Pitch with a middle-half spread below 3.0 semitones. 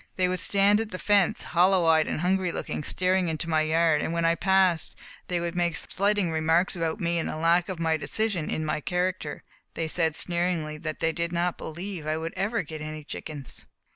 Yes: narrow, 2.5 semitones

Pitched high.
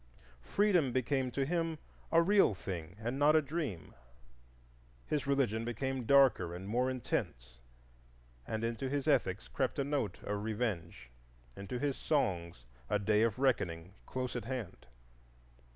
No: low, 125 Hz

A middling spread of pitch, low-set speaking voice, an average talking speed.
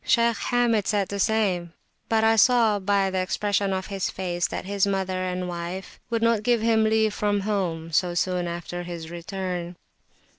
No: average, 3.4 semitones; high, 195 Hz; average, 180 wpm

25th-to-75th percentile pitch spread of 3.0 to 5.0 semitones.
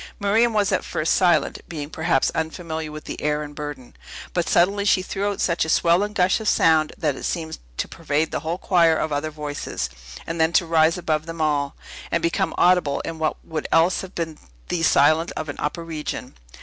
No: narrow, 2.5 semitones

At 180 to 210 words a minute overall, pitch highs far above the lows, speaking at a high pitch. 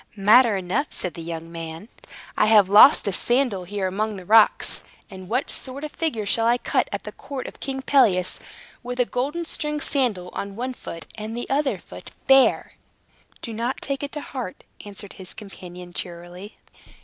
Yes: average, 185 wpm; wide, 5.9 semitones; high, 220 Hz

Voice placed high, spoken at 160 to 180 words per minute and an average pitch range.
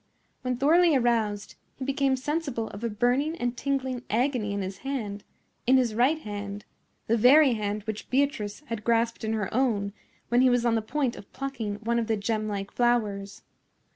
Yes: high, 235 Hz; average, 170 wpm; average, 3.9 semitones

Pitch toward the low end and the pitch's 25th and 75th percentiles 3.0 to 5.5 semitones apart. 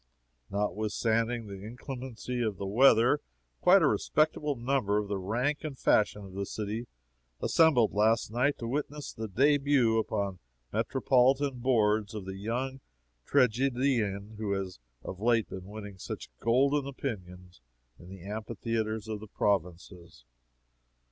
Yes: low, 110 Hz; average, 4.2 semitones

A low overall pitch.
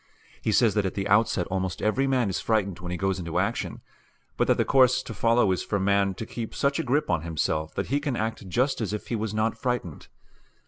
Yes: low, 105 Hz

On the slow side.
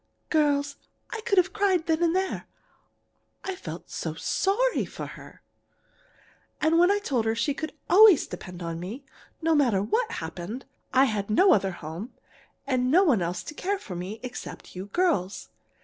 No: average, 165 wpm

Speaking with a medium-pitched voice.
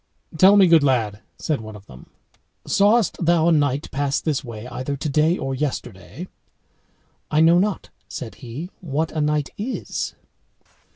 Yes: medium, 150 Hz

